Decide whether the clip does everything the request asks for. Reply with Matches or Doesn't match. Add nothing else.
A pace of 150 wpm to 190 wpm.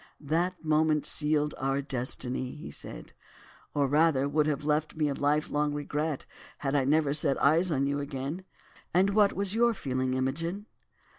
Matches